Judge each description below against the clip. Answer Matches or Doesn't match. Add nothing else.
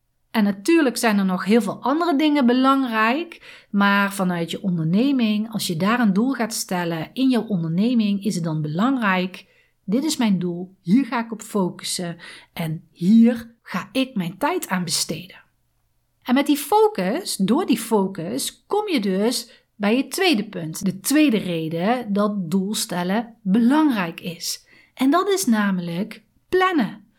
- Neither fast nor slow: Matches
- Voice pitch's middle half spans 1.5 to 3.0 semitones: Doesn't match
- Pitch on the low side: Doesn't match